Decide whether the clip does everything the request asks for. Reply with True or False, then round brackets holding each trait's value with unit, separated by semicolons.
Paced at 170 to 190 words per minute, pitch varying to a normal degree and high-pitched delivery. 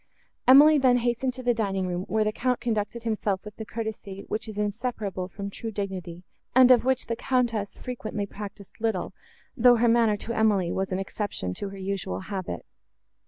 True (185 wpm; 3.3 semitones; 215 Hz)